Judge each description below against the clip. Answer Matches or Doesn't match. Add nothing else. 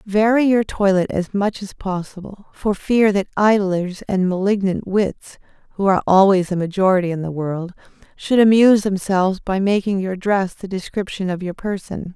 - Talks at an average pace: Matches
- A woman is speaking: Matches